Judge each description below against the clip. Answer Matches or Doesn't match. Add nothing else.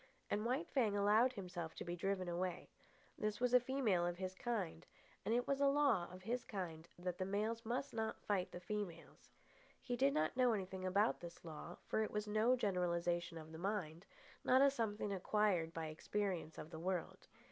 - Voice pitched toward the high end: Matches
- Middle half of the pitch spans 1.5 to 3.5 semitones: Doesn't match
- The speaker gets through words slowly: Doesn't match